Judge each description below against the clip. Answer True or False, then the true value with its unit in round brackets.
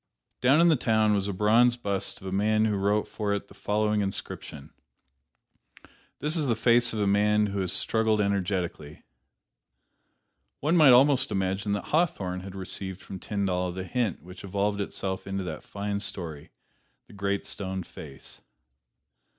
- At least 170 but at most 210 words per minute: False (160 wpm)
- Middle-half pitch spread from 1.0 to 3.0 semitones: True (2.4 semitones)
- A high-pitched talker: False (100 Hz)